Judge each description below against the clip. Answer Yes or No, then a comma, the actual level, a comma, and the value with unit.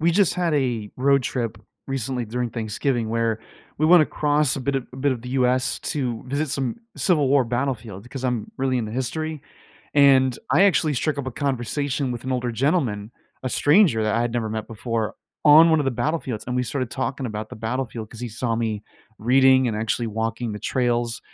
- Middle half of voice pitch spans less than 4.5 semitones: Yes, average, 3.4 semitones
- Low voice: Yes, low, 125 Hz